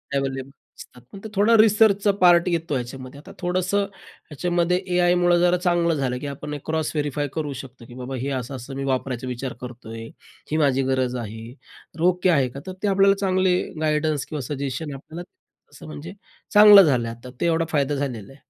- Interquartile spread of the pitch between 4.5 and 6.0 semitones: Yes, average, 5.2 semitones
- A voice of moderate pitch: Yes, medium, 145 Hz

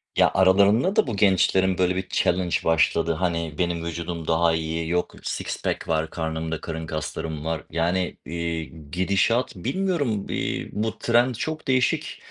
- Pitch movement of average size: Yes, average, 3.5 semitones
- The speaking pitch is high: No, very low, 85 Hz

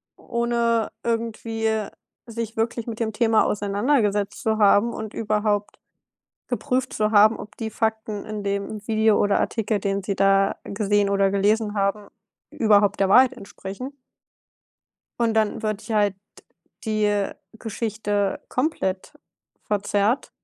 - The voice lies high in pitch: Yes, high, 215 Hz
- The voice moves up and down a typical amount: No, narrow, 1.8 semitones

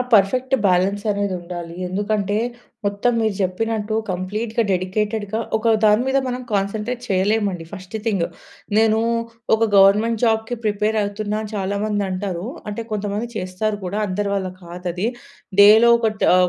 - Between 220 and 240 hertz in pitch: No, high, 205 Hz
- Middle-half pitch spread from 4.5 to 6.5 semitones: No, narrow, 2.5 semitones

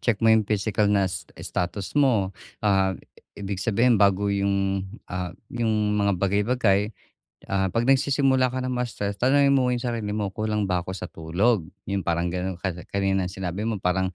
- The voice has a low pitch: Yes, low, 100 Hz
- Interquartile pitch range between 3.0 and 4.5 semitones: Yes, average, 3.3 semitones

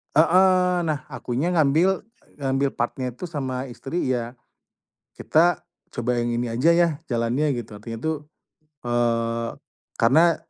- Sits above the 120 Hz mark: Yes, low, 135 Hz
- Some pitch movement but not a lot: No, wide, 5.7 semitones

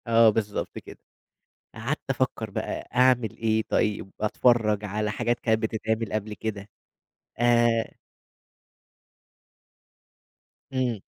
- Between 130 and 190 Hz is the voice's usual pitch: No, low, 110 Hz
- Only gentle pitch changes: Yes, narrow, 1.8 semitones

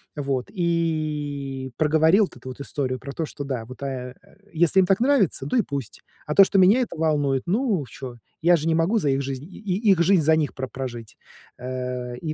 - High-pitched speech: No, medium, 150 Hz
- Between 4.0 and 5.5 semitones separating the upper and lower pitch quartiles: Yes, average, 4.5 semitones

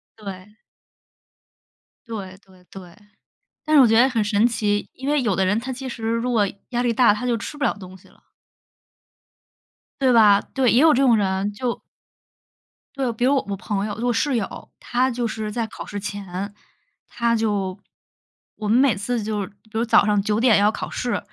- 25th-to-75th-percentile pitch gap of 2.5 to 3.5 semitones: Yes, average, 3.1 semitones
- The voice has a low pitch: No, high, 220 Hz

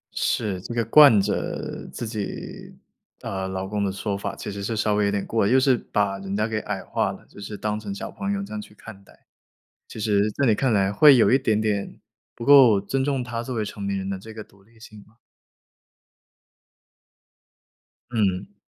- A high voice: No, low, 105 Hz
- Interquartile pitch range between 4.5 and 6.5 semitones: No, average, 2.7 semitones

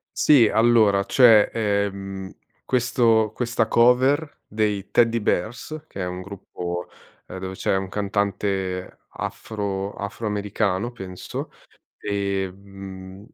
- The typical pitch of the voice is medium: No, low, 100 Hz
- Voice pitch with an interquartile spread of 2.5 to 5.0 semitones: Yes, average, 2.9 semitones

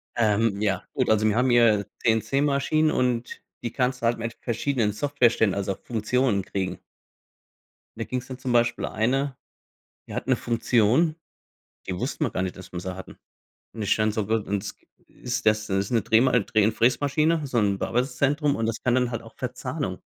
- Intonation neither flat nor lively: Yes, average, 3.3 semitones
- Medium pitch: No, low, 115 Hz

